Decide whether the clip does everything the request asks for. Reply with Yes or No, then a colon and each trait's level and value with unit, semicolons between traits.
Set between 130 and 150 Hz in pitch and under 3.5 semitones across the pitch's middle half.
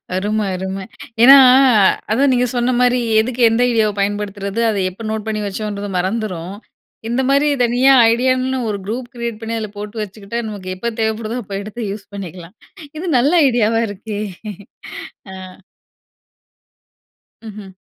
No: high, 220 Hz; average, 3.1 semitones